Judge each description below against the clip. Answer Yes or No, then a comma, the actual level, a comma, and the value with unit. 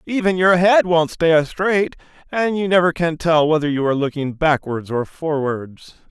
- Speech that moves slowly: No, average, 175 wpm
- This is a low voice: No, medium, 165 Hz